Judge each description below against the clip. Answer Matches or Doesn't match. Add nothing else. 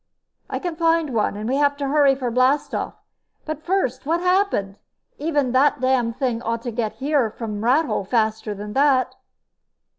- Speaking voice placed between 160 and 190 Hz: Doesn't match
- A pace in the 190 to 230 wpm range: Doesn't match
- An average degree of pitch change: Matches